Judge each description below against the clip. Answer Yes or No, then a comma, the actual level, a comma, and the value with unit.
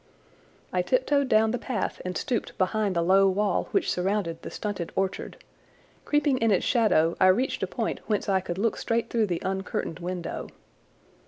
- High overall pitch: Yes, high, 200 Hz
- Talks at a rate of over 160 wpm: Yes, average, 175 wpm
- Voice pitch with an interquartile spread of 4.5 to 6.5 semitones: No, average, 3.7 semitones